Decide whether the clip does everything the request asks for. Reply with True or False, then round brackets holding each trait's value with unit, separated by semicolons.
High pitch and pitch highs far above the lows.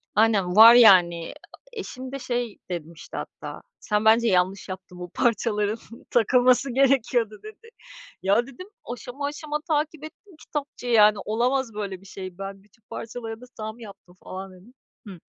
False (225 Hz; 4.4 semitones)